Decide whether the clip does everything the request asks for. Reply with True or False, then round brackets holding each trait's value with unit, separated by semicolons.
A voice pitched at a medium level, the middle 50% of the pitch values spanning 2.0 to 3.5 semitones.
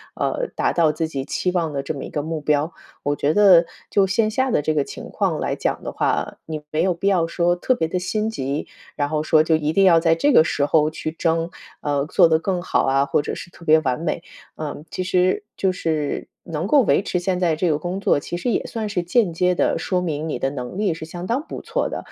True (165 Hz; 3.2 semitones)